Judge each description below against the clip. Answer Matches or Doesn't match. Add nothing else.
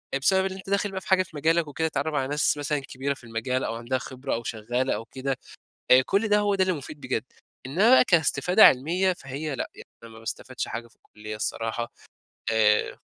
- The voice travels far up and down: Matches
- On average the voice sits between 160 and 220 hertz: Doesn't match